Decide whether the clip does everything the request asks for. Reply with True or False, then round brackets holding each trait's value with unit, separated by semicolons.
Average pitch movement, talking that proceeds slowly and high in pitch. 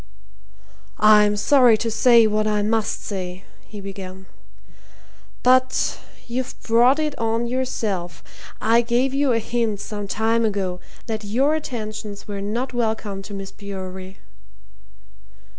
True (3.0 semitones; 125 wpm; 215 Hz)